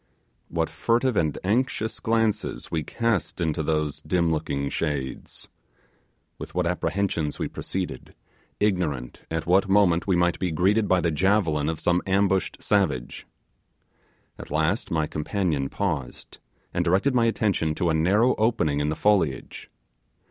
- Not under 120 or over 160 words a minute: Yes, average, 140 wpm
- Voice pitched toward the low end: Yes, very low, 90 Hz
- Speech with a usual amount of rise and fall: Yes, average, 4.7 semitones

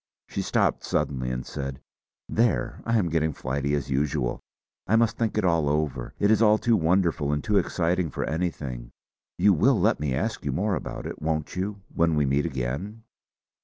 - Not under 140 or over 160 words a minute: No, average, 190 wpm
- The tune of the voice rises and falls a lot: Yes, wide, 6.4 semitones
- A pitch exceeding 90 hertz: No, very low, 80 Hz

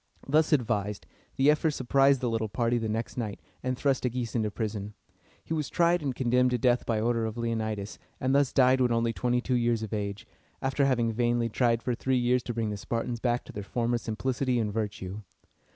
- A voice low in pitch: Yes, low, 120 Hz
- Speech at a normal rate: No, fast, 210 wpm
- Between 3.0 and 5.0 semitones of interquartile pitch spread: No, narrow, 2.6 semitones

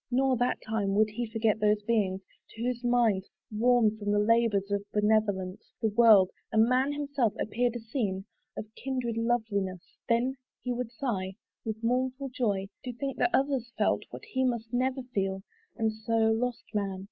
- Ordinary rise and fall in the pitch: Yes, average, 3.0 semitones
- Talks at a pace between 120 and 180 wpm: Yes, average, 170 wpm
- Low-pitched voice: No, high, 225 Hz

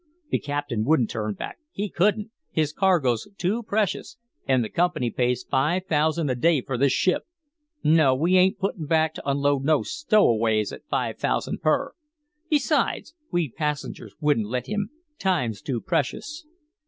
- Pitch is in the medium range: Yes, medium, 150 Hz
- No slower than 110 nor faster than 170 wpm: Yes, average, 155 wpm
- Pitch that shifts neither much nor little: No, wide, 6.4 semitones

